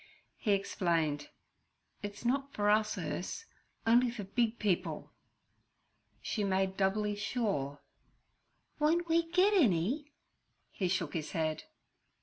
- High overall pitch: Yes, high, 210 Hz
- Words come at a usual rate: No, slow, 110 wpm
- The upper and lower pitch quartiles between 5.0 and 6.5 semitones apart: Yes, wide, 5.4 semitones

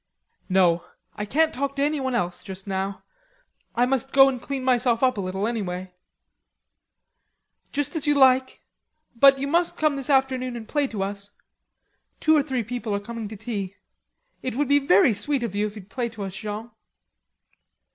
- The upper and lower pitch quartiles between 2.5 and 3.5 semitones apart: No, average, 5.1 semitones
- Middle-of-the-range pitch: No, high, 240 Hz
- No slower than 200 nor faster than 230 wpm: No, average, 175 wpm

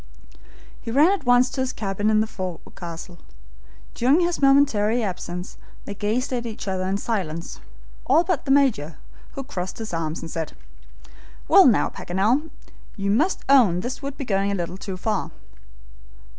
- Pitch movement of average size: No, wide, 6.3 semitones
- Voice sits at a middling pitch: No, high, 215 Hz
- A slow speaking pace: No, average, 165 wpm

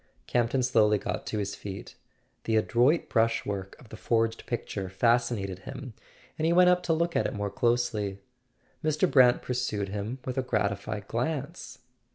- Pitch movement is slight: No, average, 4.0 semitones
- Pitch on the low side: Yes, low, 115 Hz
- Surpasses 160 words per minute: Yes, average, 170 wpm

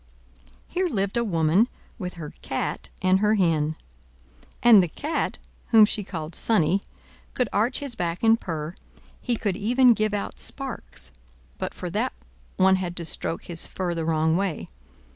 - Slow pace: No, average, 160 wpm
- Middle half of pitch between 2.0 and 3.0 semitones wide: No, average, 5.2 semitones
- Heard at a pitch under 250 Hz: Yes, high, 190 Hz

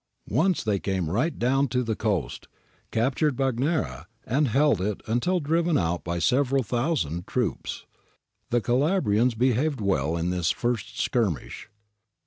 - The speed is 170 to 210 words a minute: No, average, 140 wpm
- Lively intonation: Yes, wide, 6.4 semitones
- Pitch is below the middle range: Yes, low, 120 Hz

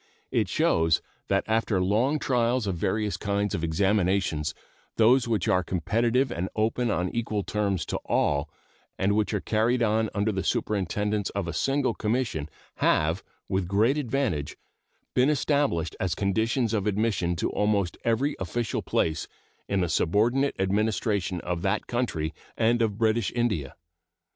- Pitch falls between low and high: No, low, 105 Hz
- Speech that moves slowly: No, average, 150 wpm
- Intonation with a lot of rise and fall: No, average, 4.0 semitones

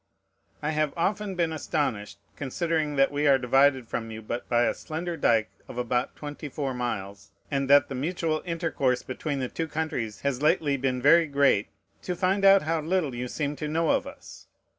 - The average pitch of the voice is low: No, medium, 145 Hz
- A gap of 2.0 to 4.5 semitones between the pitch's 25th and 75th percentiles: Yes, average, 4.2 semitones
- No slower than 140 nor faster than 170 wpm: No, average, 185 wpm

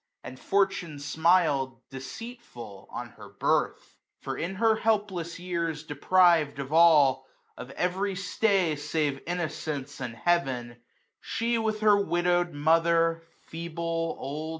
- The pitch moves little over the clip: No, average, 4.1 semitones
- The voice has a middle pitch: Yes, medium, 165 Hz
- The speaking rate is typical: No, slow, 125 wpm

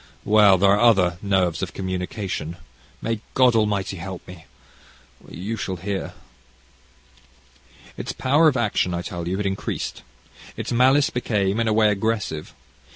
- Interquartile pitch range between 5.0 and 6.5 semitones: No, average, 3.5 semitones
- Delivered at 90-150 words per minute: Yes, average, 145 wpm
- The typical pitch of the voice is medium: No, low, 100 Hz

